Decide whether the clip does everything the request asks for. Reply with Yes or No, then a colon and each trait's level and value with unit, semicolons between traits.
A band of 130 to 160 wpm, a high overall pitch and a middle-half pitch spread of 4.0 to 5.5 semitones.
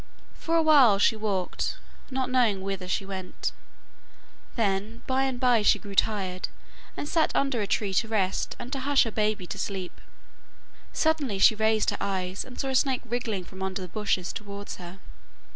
No: average, 180 wpm; high, 215 Hz; average, 4.7 semitones